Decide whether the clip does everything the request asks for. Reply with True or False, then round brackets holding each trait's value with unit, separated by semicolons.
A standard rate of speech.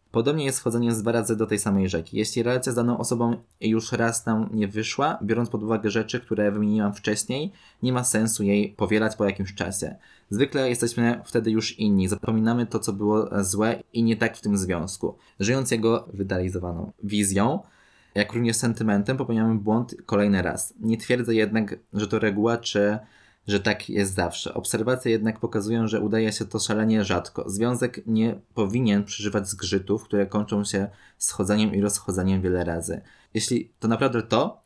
False (170 wpm)